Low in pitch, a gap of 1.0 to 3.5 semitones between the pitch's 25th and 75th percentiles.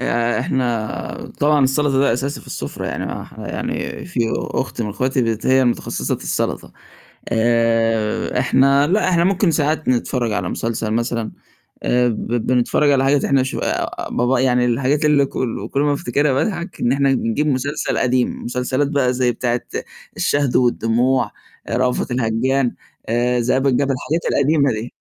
Yes: low, 130 Hz; average, 2.9 semitones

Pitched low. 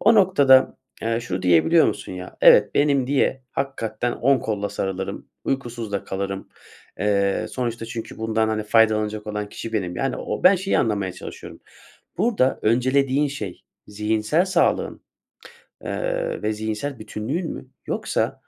Yes: low, 115 Hz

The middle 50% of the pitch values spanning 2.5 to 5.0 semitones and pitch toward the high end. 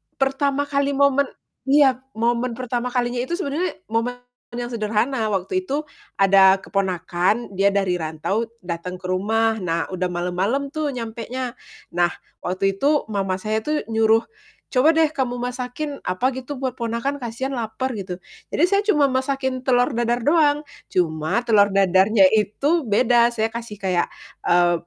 No: wide, 5.6 semitones; high, 235 Hz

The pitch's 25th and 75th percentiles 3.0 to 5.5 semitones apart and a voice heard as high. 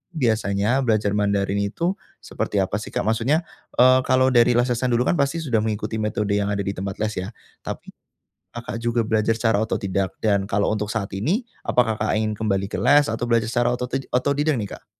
No: average, 3.3 semitones; low, 110 Hz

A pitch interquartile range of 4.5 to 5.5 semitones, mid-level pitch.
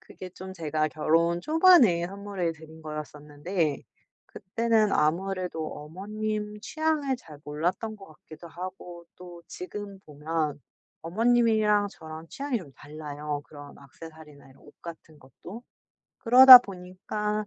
Yes: average, 5.2 semitones; medium, 175 Hz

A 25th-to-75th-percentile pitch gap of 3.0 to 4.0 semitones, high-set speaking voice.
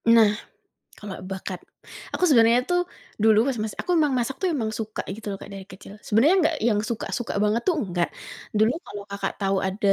Yes: average, 3.5 semitones; high, 220 Hz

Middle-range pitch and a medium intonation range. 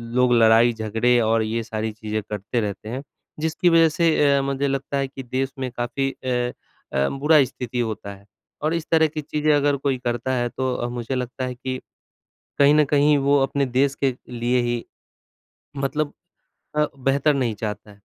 No: low, 130 Hz; average, 3.3 semitones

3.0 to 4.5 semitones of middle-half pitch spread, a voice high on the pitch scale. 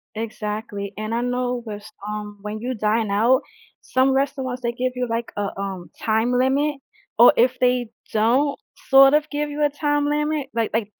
Yes: average, 3.9 semitones; high, 245 Hz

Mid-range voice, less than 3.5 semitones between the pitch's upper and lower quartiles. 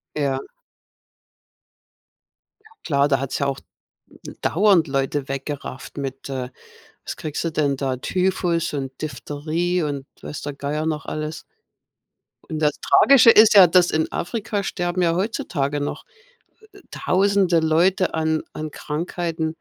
No: medium, 155 Hz; average, 3.8 semitones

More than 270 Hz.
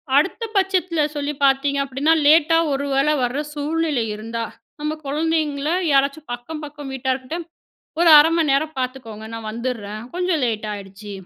Yes: very high, 280 Hz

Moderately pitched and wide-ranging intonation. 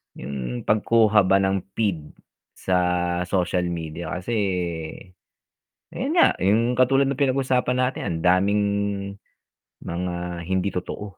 No: low, 100 Hz; wide, 5.9 semitones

